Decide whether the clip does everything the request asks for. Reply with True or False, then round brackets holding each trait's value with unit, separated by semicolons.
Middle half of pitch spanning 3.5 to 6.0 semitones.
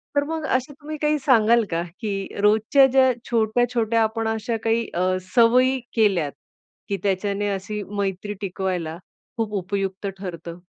True (3.8 semitones)